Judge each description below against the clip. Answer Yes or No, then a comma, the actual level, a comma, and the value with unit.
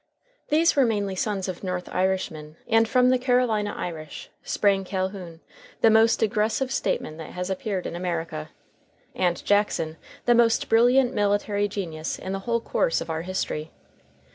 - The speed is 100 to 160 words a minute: Yes, average, 155 wpm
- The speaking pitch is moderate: No, high, 200 Hz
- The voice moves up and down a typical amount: Yes, average, 4.0 semitones